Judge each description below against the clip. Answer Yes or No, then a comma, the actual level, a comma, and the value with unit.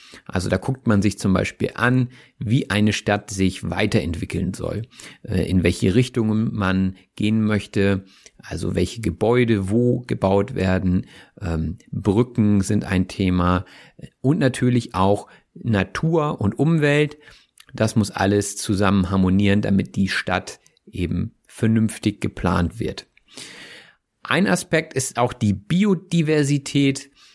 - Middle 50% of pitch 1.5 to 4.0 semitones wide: No, average, 4.6 semitones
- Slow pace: Yes, slow, 120 wpm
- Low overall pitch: Yes, low, 105 Hz